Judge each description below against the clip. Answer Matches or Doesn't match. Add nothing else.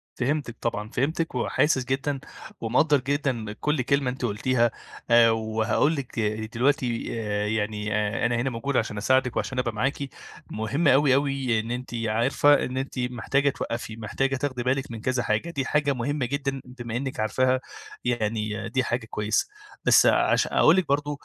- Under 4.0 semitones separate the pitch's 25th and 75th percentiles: Matches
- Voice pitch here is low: Matches